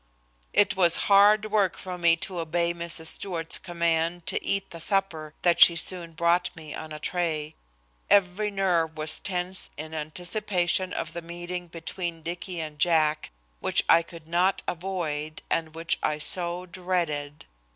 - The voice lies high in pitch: No, medium, 170 Hz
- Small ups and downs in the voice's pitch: Yes, narrow, 2.1 semitones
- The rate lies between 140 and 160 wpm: Yes, average, 155 wpm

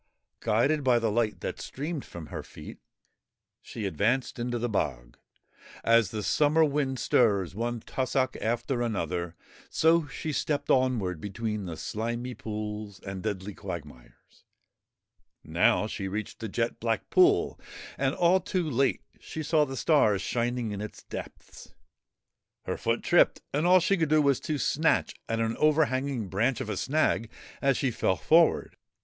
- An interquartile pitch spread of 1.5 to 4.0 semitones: No, average, 5.3 semitones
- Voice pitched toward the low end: Yes, low, 120 Hz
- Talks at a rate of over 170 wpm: No, average, 155 wpm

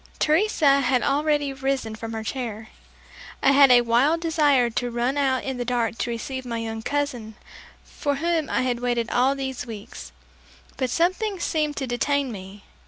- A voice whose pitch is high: Yes, very high, 260 Hz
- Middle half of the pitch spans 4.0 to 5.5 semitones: No, average, 3.4 semitones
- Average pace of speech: Yes, average, 170 wpm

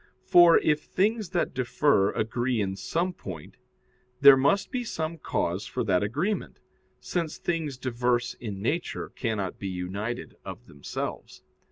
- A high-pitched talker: No, low, 130 Hz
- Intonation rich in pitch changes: Yes, wide, 8.3 semitones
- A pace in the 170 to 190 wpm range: No, average, 140 wpm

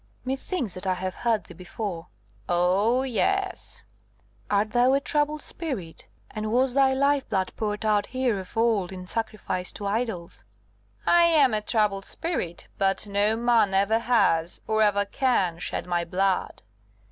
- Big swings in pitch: No, average, 4.9 semitones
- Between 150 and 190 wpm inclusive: Yes, average, 155 wpm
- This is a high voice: Yes, high, 215 Hz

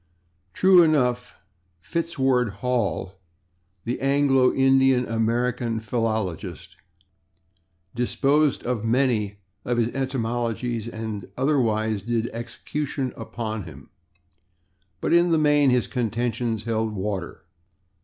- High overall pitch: No, low, 120 Hz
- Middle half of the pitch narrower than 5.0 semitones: Yes, average, 3.2 semitones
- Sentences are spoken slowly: Yes, slow, 95 wpm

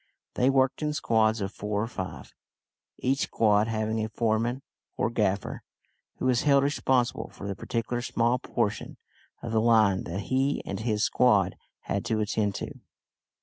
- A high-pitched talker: No, low, 115 Hz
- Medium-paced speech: Yes, average, 160 wpm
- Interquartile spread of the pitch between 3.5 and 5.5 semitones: No, average, 3.1 semitones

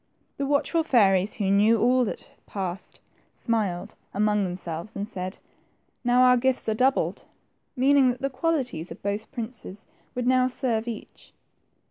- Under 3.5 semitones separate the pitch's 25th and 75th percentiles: No, average, 4.3 semitones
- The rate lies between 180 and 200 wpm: No, average, 165 wpm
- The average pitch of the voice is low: No, high, 230 Hz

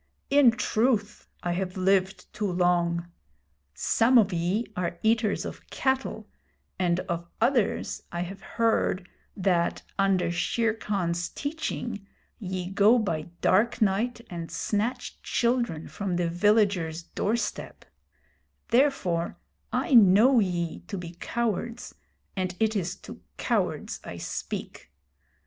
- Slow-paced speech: Yes, slow, 125 wpm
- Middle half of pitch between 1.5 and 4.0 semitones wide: No, average, 4.4 semitones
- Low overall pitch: No, high, 195 Hz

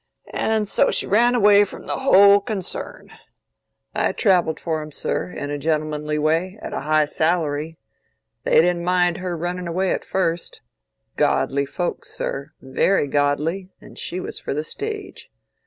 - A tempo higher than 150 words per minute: No, average, 145 wpm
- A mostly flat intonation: No, average, 4.0 semitones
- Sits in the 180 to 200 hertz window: No, medium, 170 Hz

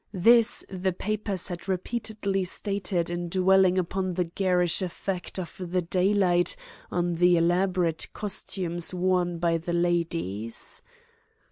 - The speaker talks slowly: Yes, slow, 120 wpm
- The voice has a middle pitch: Yes, medium, 180 Hz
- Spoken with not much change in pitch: Yes, narrow, 1.8 semitones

